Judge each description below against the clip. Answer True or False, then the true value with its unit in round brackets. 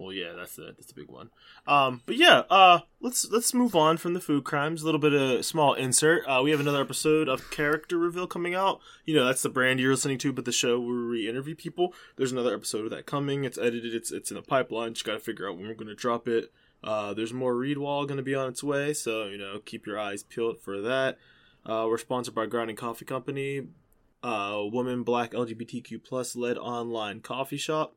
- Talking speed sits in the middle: False (235 wpm)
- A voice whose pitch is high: False (130 Hz)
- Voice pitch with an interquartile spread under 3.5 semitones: False (4.4 semitones)